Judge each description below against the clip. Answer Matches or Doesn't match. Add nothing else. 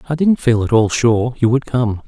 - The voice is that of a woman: Doesn't match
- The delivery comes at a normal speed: Doesn't match